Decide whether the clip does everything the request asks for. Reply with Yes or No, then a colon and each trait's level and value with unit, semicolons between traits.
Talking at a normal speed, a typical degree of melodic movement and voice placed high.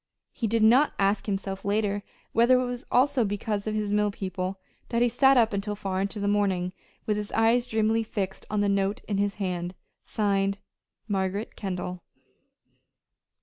No: average, 170 wpm; narrow, 2.3 semitones; high, 205 Hz